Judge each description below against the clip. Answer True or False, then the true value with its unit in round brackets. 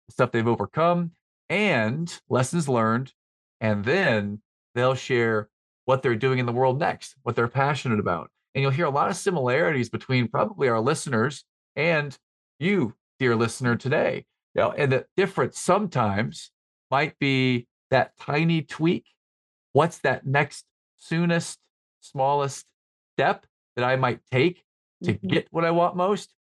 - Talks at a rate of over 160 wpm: False (145 wpm)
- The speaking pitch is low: True (130 Hz)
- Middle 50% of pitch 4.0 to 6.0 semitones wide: True (4.9 semitones)